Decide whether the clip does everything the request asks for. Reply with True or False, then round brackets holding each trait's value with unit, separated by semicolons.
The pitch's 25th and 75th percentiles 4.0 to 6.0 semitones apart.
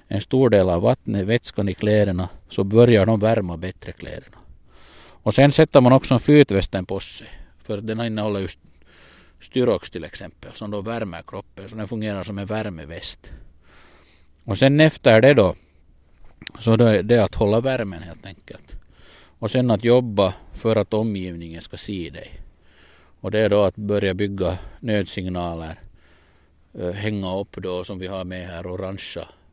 True (4.4 semitones)